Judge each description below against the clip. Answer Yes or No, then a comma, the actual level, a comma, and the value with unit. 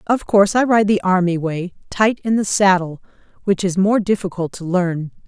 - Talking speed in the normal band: Yes, average, 195 wpm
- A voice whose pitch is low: No, high, 190 Hz